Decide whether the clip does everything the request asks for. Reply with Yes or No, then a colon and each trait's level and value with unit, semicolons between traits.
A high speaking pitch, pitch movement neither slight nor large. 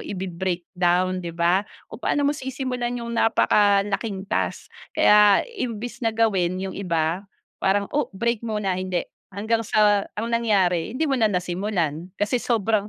Yes: high, 205 Hz; average, 3.7 semitones